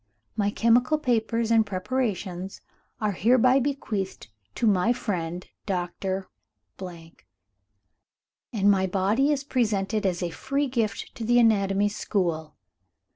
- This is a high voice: Yes, high, 205 Hz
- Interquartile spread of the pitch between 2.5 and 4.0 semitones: No, average, 4.4 semitones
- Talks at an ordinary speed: No, slow, 115 wpm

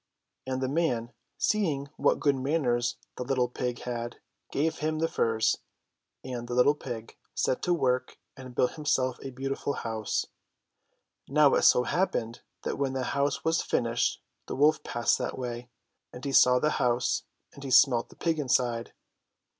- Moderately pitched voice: No, low, 130 Hz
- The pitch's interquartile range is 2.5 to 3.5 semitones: Yes, average, 2.8 semitones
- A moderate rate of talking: Yes, average, 165 wpm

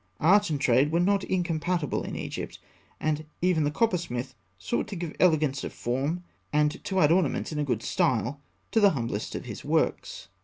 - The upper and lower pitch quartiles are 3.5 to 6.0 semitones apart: Yes, average, 4.7 semitones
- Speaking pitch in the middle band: Yes, medium, 155 Hz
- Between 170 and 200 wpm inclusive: Yes, average, 185 wpm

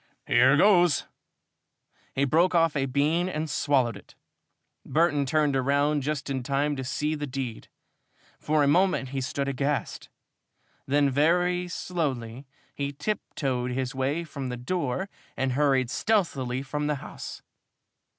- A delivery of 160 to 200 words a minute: No, average, 140 wpm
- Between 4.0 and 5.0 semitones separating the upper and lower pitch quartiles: No, average, 2.9 semitones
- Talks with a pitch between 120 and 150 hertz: Yes, medium, 140 Hz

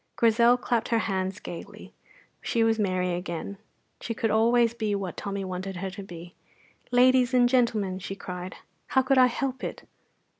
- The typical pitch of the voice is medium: No, high, 215 Hz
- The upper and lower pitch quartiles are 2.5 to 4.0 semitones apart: No, average, 4.4 semitones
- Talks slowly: No, average, 165 wpm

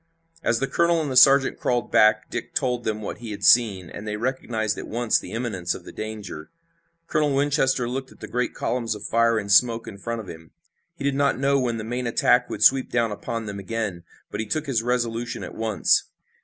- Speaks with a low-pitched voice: Yes, low, 115 Hz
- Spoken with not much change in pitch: No, average, 3.1 semitones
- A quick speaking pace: Yes, fast, 225 wpm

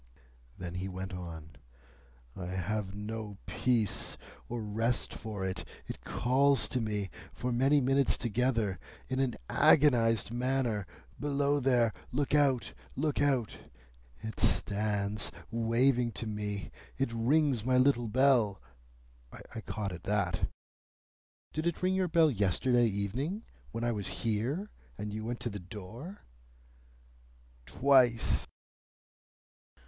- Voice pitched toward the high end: No, low, 115 Hz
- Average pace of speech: No, slow, 125 wpm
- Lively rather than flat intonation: No, average, 4.4 semitones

